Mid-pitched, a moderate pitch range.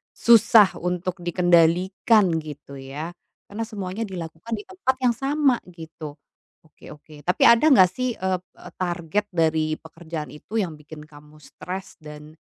Yes: medium, 175 Hz; average, 4.8 semitones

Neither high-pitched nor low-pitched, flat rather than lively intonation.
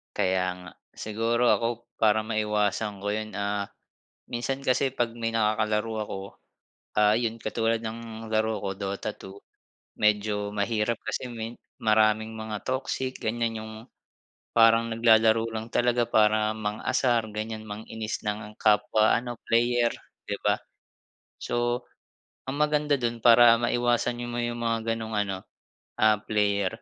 No: low, 110 Hz; narrow, 1.8 semitones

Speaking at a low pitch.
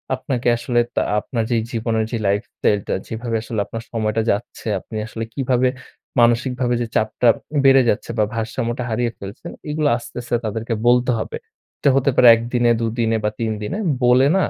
Yes: low, 120 Hz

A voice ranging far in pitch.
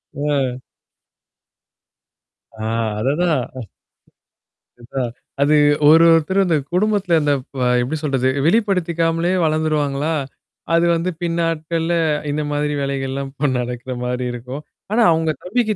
No: average, 3.7 semitones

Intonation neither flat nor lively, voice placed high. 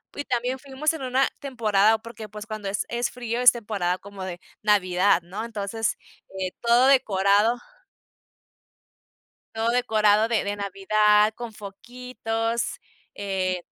Yes: average, 3.1 semitones; high, 215 Hz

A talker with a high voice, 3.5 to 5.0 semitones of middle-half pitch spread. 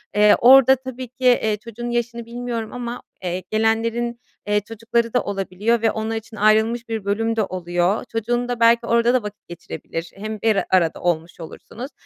No: high, 225 Hz; narrow, 2.4 semitones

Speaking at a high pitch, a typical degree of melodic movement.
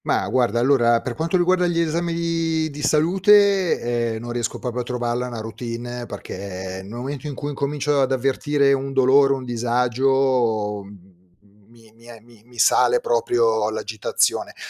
No: low, 125 Hz; average, 4.6 semitones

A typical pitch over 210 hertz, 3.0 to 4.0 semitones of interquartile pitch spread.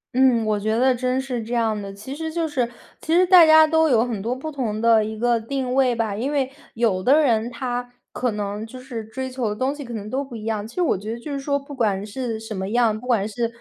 Yes: high, 240 Hz; average, 3.4 semitones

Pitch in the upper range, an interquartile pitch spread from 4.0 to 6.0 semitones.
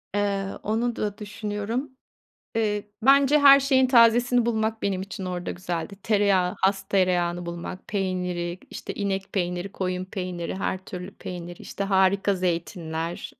No: high, 195 Hz; average, 3.1 semitones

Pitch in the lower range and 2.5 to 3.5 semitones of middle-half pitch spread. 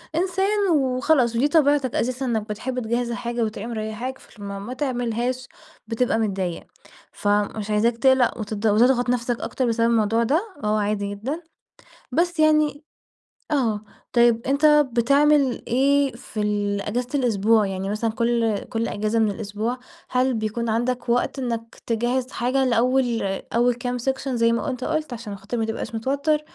No: high, 240 Hz; average, 3.1 semitones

